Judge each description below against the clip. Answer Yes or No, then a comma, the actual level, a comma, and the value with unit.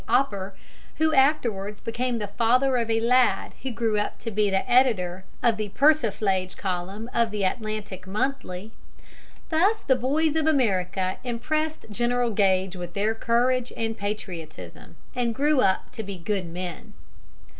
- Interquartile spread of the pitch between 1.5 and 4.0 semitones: No, average, 4.7 semitones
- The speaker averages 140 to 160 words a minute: Yes, average, 145 wpm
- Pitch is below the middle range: No, high, 225 Hz